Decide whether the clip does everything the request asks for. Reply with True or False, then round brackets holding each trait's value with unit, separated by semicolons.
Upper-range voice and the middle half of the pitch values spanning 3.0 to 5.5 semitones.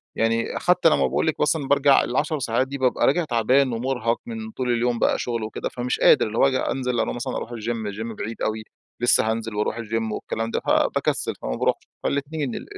False (120 Hz; 3.5 semitones)